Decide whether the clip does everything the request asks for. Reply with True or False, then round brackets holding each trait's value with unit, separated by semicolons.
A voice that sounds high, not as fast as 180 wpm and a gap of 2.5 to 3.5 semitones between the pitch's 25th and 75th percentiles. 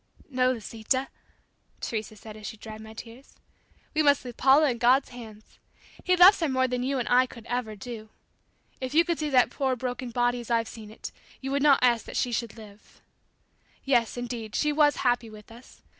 False (245 Hz; 205 wpm; 3.0 semitones)